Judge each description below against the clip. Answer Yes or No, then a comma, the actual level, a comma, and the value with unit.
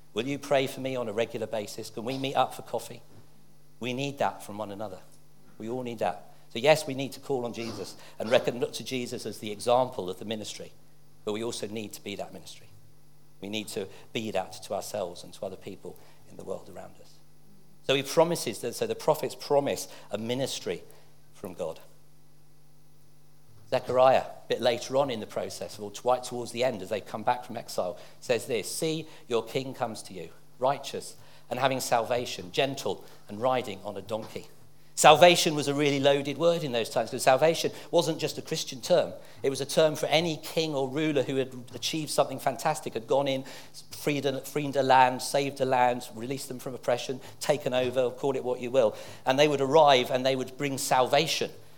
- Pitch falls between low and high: No, low, 130 Hz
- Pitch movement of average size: Yes, average, 3.2 semitones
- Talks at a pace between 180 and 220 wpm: Yes, fast, 205 wpm